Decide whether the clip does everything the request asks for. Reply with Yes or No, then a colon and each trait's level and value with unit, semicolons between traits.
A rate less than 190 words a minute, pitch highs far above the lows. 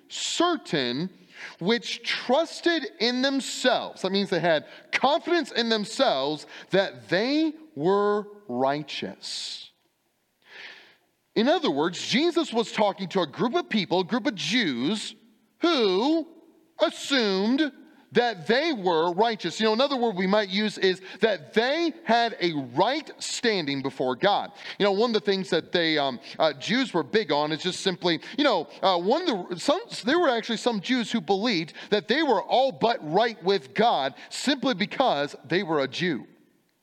Yes: average, 160 wpm; wide, 6.3 semitones